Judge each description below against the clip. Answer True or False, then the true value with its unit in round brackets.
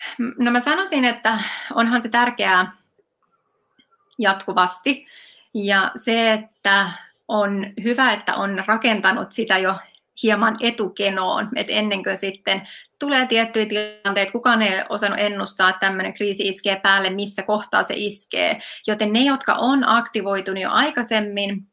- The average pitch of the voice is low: False (215 Hz)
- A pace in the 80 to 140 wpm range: True (130 wpm)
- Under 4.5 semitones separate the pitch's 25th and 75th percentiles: True (3.3 semitones)